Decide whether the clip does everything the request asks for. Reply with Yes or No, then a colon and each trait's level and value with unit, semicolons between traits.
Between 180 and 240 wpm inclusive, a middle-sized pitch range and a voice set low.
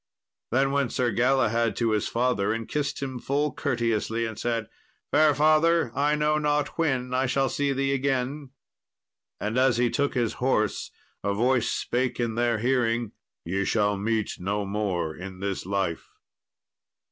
No: average, 160 wpm; average, 4.1 semitones; low, 120 Hz